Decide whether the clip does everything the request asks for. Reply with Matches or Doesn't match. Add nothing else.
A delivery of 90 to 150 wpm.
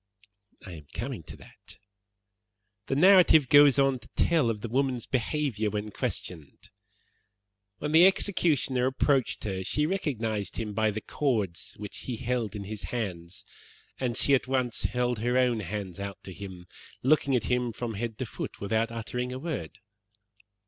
Doesn't match